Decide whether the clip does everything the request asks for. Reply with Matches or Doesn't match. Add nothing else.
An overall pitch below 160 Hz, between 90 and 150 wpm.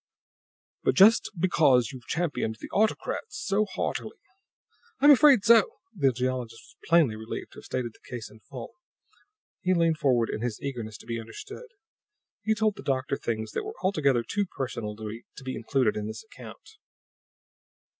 Doesn't match